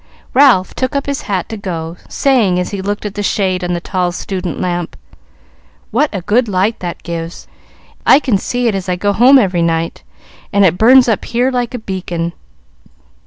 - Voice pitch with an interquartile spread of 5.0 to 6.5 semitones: Yes, average, 5.3 semitones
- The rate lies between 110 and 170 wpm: No, average, 195 wpm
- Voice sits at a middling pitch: No, high, 195 Hz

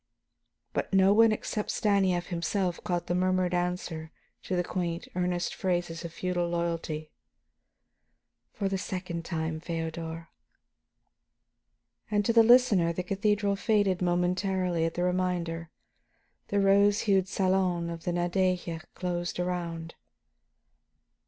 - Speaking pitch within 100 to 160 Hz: No, medium, 180 Hz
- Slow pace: Yes, slow, 120 wpm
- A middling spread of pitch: No, narrow, 2.2 semitones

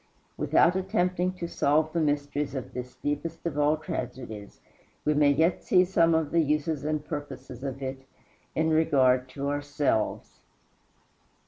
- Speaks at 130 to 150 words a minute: Yes, average, 145 wpm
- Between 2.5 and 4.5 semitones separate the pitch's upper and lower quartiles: Yes, average, 2.8 semitones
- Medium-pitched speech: Yes, medium, 150 Hz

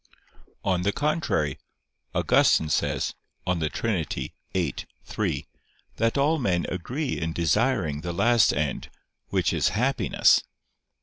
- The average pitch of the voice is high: No, very low, 95 Hz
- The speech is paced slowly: Yes, slow, 115 wpm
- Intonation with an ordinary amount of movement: No, wide, 7.0 semitones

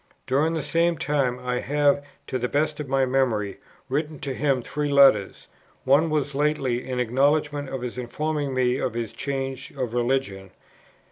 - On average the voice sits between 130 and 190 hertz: Yes, low, 135 Hz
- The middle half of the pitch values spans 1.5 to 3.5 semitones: Yes, average, 2.8 semitones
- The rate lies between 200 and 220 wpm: No, average, 165 wpm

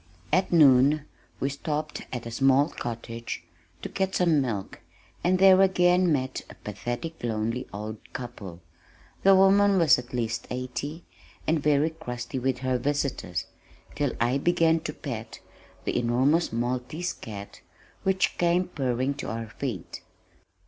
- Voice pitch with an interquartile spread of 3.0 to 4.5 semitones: No, average, 5.3 semitones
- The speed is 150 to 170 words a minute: No, average, 140 wpm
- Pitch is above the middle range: No, low, 135 Hz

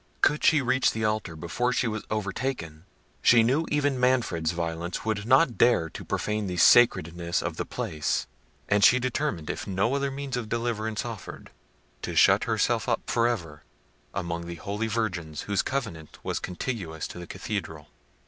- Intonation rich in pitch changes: Yes, wide, 6.4 semitones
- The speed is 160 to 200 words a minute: Yes, average, 165 wpm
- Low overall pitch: Yes, low, 110 Hz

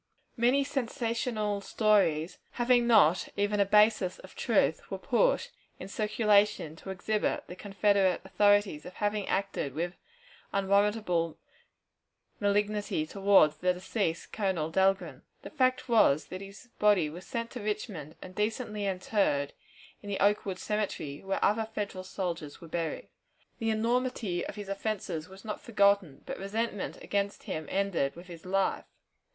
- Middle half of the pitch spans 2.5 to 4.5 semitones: Yes, average, 2.8 semitones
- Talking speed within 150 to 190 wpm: No, average, 140 wpm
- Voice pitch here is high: Yes, high, 200 Hz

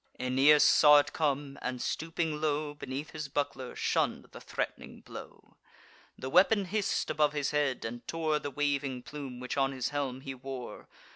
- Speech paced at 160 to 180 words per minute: Yes, average, 165 wpm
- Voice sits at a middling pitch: Yes, medium, 145 Hz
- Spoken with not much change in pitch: Yes, narrow, 2.3 semitones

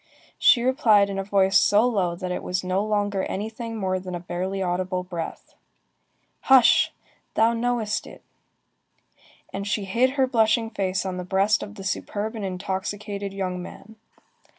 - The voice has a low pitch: No, high, 200 Hz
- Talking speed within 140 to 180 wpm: Yes, average, 160 wpm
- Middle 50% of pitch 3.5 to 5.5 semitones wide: No, average, 2.9 semitones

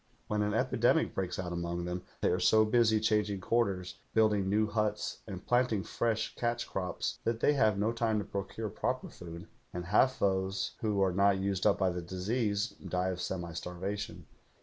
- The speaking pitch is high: No, low, 100 Hz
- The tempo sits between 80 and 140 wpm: No, average, 185 wpm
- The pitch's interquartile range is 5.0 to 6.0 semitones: No, average, 3.2 semitones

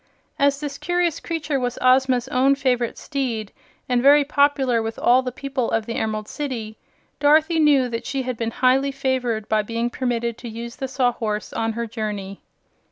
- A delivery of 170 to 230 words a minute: Yes, average, 175 wpm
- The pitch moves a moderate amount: Yes, average, 3.3 semitones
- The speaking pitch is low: No, very high, 250 Hz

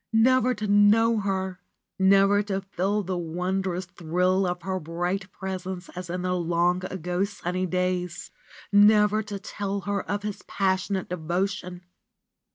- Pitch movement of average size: No, narrow, 2.1 semitones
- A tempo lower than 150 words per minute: Yes, average, 140 wpm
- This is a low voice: No, high, 190 Hz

